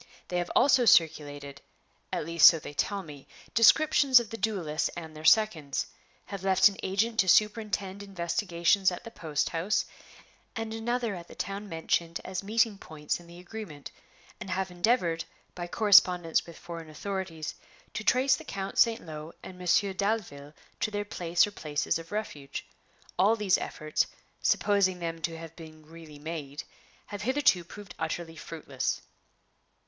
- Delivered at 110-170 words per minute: Yes, average, 160 wpm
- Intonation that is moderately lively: Yes, average, 4.2 semitones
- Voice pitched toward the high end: No, medium, 180 Hz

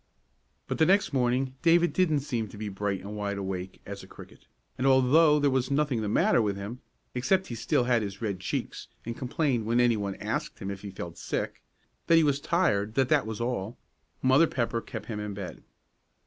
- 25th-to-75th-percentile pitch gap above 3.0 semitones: Yes, average, 5.1 semitones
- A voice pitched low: Yes, low, 120 Hz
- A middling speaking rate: No, fast, 210 wpm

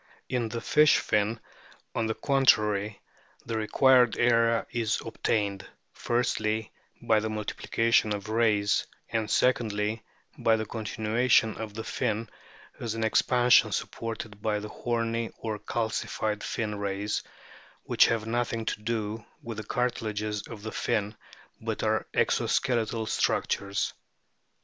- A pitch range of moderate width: No, narrow, 1.6 semitones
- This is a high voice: No, low, 110 Hz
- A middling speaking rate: No, slow, 125 wpm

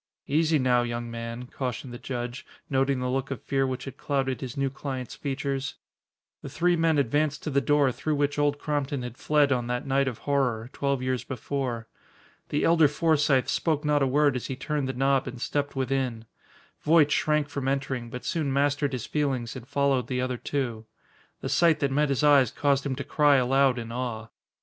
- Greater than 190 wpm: Yes, average, 200 wpm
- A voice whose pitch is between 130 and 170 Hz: Yes, low, 135 Hz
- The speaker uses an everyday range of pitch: No, narrow, 2.3 semitones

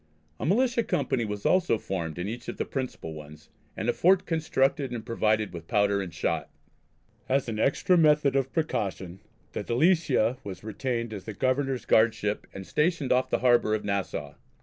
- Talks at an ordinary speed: Yes, average, 175 wpm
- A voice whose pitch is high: No, low, 120 Hz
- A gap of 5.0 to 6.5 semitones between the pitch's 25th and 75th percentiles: Yes, average, 5.3 semitones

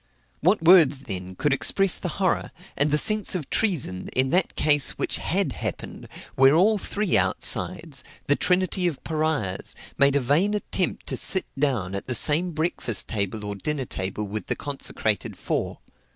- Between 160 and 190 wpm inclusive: Yes, average, 165 wpm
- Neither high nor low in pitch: Yes, medium, 145 Hz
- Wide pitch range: Yes, wide, 6.8 semitones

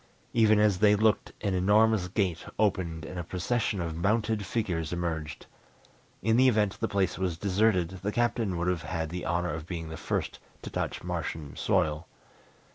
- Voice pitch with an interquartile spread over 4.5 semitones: No, average, 4.1 semitones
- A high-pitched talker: No, very low, 95 Hz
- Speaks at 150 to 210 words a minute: Yes, average, 175 wpm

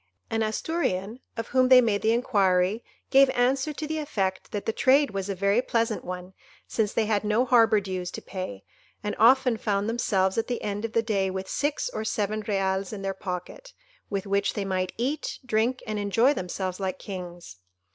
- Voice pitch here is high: Yes, high, 210 Hz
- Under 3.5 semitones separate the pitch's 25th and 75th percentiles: No, average, 3.9 semitones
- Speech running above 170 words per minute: Yes, average, 195 wpm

